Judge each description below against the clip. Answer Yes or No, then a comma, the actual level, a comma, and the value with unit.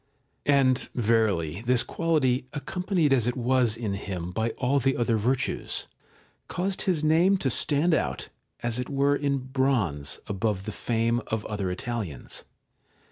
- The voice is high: No, low, 125 Hz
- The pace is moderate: Yes, average, 145 wpm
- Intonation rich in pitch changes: No, average, 4.4 semitones